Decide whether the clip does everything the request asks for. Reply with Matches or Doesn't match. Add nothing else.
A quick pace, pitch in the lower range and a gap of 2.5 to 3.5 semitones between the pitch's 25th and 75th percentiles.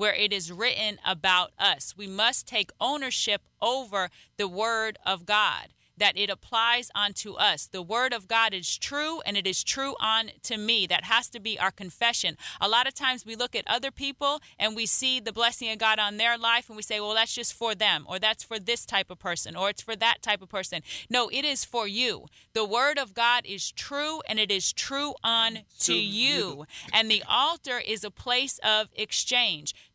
Doesn't match